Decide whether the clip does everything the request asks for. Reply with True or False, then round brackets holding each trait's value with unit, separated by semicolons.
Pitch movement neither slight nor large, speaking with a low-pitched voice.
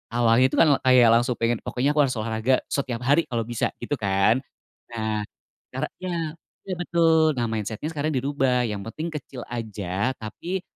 True (4.3 semitones; 120 Hz)